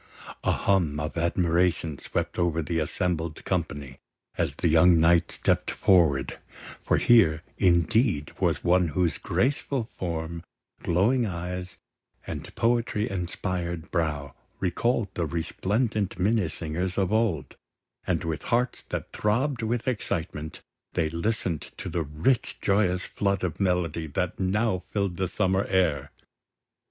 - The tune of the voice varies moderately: Yes, average, 3.7 semitones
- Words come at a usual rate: No, slow, 125 wpm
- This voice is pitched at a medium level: No, very low, 90 Hz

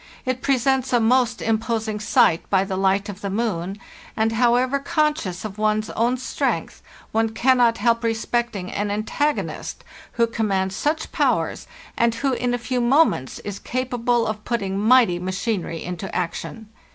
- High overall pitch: Yes, high, 225 Hz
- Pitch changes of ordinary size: Yes, average, 3.5 semitones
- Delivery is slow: No, average, 150 wpm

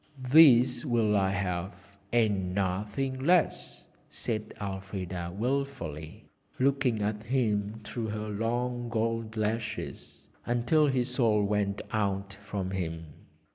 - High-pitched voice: No, low, 110 Hz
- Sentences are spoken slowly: Yes, slow, 110 wpm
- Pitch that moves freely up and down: No, average, 3.7 semitones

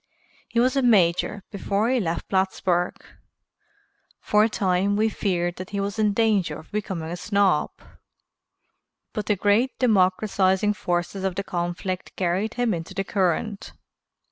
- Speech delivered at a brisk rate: No, average, 145 wpm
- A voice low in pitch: No, high, 195 Hz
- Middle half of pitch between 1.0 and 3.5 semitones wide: Yes, average, 2.8 semitones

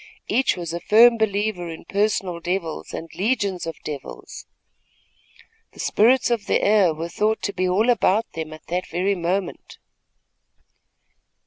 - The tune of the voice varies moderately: Yes, average, 4.1 semitones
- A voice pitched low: No, high, 190 Hz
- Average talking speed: Yes, average, 150 wpm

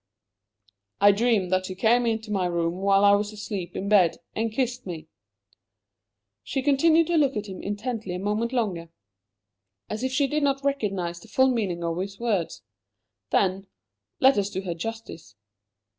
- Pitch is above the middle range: Yes, high, 205 Hz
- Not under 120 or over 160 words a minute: No, average, 170 wpm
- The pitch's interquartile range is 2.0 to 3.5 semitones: No, average, 4.7 semitones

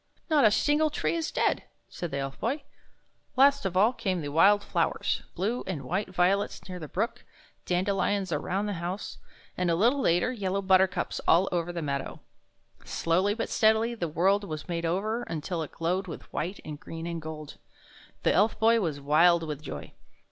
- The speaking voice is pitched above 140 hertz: Yes, medium, 185 Hz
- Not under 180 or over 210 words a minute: Yes, average, 190 wpm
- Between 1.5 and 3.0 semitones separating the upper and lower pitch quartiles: No, average, 4.1 semitones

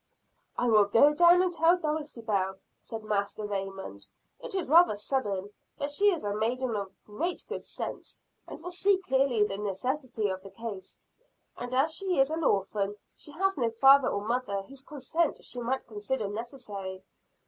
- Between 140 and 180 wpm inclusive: Yes, average, 170 wpm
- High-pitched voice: Yes, high, 240 Hz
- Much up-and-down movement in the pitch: Yes, wide, 6.6 semitones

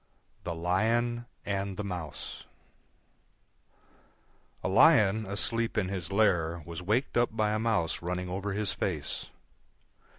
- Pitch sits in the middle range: No, low, 100 Hz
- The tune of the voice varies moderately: Yes, average, 3.7 semitones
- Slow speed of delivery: Yes, slow, 125 wpm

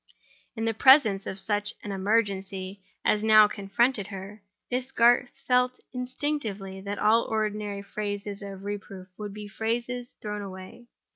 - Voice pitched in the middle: No, high, 210 Hz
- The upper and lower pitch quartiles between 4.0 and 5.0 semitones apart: No, average, 2.7 semitones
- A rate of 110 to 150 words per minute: Yes, average, 140 wpm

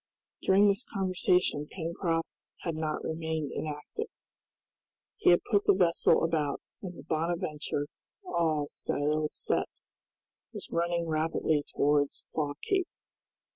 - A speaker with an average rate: No, slow, 115 wpm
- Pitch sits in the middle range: Yes, medium, 160 Hz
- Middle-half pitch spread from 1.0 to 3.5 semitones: Yes, narrow, 2.6 semitones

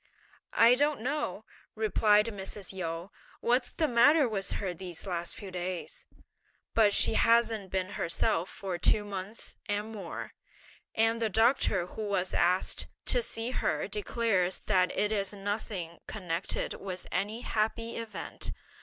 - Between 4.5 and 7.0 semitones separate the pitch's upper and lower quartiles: No, average, 3.5 semitones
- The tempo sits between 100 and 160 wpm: Yes, average, 140 wpm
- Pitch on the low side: No, high, 205 Hz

